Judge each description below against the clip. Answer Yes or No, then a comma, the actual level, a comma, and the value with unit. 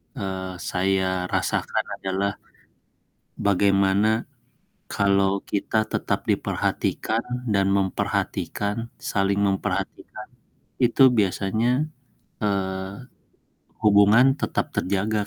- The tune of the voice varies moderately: No, narrow, 2.0 semitones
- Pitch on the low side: Yes, low, 100 Hz